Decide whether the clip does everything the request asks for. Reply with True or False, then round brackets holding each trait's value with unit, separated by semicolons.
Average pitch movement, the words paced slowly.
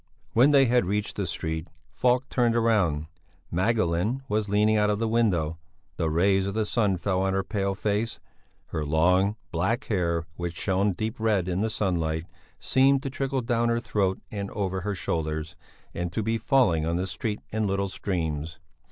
False (4.4 semitones; 180 wpm)